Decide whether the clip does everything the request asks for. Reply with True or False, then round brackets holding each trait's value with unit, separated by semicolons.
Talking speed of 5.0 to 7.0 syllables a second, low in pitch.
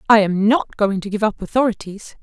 False (5.5 syllables/s; 210 Hz)